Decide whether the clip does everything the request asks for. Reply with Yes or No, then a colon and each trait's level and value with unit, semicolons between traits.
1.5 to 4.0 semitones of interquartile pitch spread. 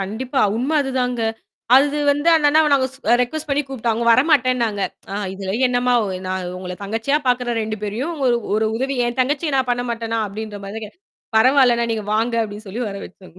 Yes: average, 3.7 semitones